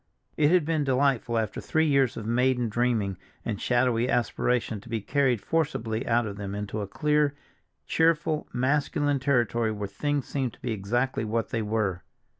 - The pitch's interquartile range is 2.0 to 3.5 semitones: No, average, 4.3 semitones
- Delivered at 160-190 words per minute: Yes, average, 170 wpm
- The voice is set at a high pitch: No, low, 120 Hz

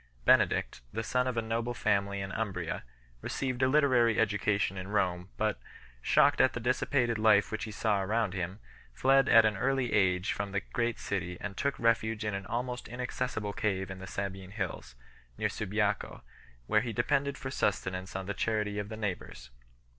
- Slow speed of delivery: No, average, 180 wpm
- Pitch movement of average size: Yes, average, 3.4 semitones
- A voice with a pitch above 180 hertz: No, low, 105 Hz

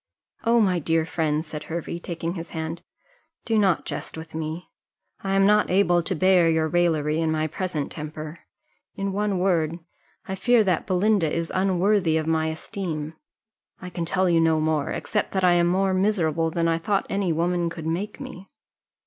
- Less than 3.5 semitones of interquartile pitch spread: Yes, average, 3.1 semitones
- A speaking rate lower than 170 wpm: No, average, 185 wpm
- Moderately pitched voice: Yes, medium, 170 Hz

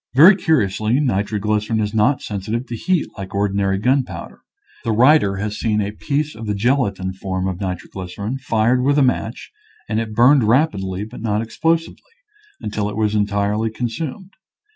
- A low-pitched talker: Yes, low, 110 Hz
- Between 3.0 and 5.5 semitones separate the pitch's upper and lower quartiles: Yes, average, 4.0 semitones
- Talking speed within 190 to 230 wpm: No, average, 165 wpm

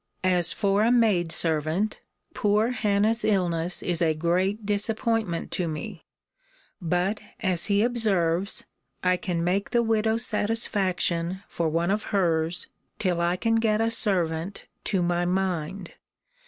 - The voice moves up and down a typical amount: Yes, average, 3.8 semitones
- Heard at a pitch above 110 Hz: Yes, high, 190 Hz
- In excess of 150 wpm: No, slow, 135 wpm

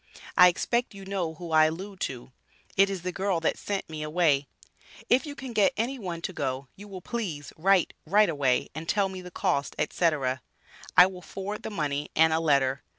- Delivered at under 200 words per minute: No, fast, 205 wpm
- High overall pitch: No, medium, 180 Hz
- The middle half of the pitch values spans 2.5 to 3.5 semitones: No, average, 4.1 semitones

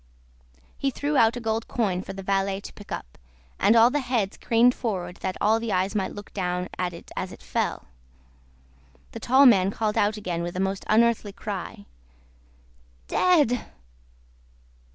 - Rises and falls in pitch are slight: No, average, 3.7 semitones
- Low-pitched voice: No, high, 210 Hz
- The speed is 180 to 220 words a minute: No, average, 170 wpm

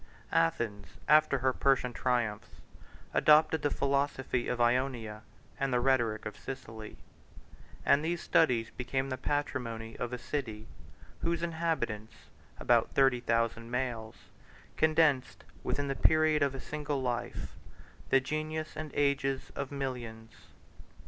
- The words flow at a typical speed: No, slow, 125 wpm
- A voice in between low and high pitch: No, low, 130 Hz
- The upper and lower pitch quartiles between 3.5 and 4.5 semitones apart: Yes, average, 3.8 semitones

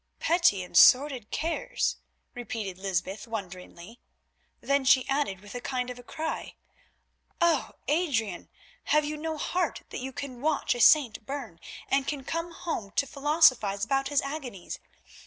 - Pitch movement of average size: No, wide, 5.8 semitones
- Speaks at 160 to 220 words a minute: No, average, 140 wpm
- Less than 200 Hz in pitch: No, very high, 265 Hz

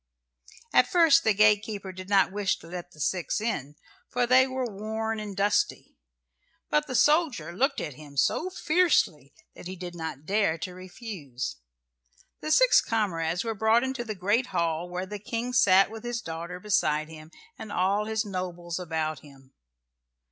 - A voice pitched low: No, high, 200 Hz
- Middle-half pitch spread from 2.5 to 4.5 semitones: No, average, 5.0 semitones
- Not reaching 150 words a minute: No, average, 170 wpm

